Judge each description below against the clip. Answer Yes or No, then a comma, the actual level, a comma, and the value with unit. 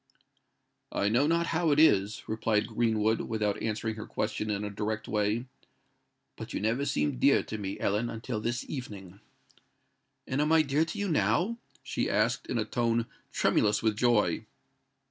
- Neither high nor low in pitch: No, low, 110 Hz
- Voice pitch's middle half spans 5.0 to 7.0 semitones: No, average, 3.3 semitones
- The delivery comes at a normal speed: Yes, average, 165 wpm